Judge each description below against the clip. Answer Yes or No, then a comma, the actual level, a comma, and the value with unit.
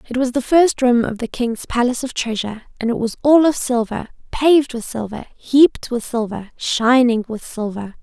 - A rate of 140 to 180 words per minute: No, average, 195 wpm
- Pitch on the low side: No, high, 245 Hz